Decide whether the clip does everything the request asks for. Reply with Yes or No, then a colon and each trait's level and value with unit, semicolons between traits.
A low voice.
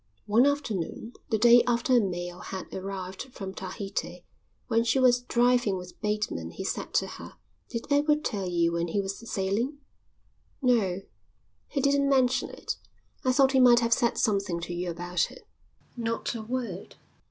No: high, 220 Hz